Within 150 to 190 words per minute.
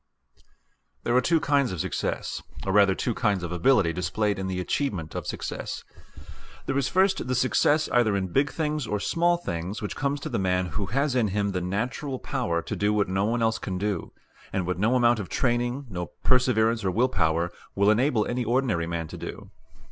No: fast, 205 wpm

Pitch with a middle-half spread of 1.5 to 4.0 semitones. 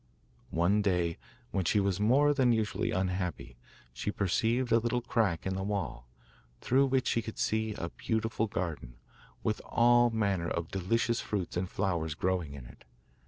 No: average, 4.6 semitones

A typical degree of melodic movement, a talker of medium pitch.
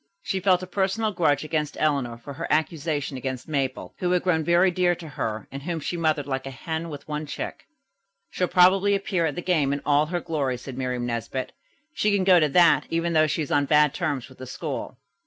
Yes: average, 4.2 semitones; medium, 155 Hz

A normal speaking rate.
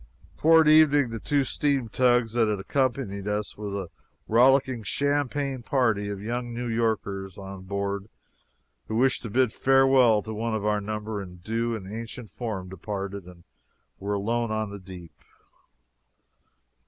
Yes: average, 155 wpm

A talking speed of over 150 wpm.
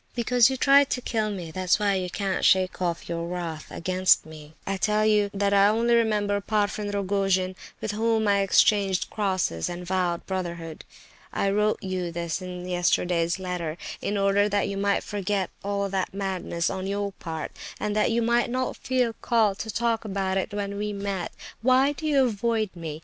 Yes: average, 185 wpm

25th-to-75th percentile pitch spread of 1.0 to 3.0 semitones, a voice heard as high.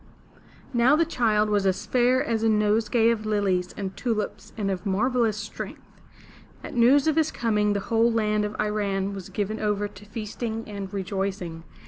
Yes: narrow, 2.4 semitones; high, 210 Hz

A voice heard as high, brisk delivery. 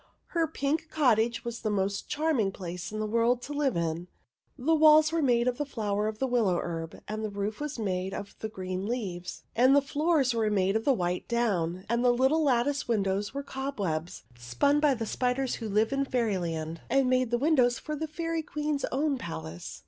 Yes: high, 235 Hz; fast, 210 wpm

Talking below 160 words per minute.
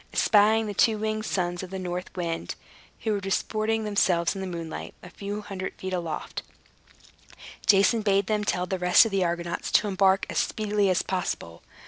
No: average, 180 wpm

